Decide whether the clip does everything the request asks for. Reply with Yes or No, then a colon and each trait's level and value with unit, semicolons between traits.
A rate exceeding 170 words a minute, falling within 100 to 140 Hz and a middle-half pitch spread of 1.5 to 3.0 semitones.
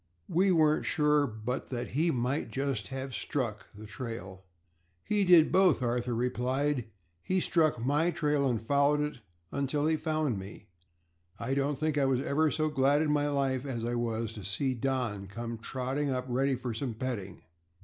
No: average, 180 wpm; low, 135 Hz; average, 3.8 semitones